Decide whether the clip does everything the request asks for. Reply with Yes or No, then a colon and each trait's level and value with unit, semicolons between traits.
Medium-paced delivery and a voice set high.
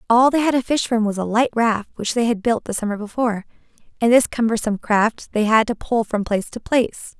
No: fast, 240 wpm; high, 225 Hz